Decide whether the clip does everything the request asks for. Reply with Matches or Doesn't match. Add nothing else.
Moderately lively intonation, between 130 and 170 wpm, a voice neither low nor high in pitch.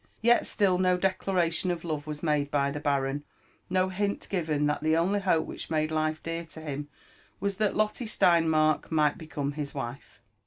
Doesn't match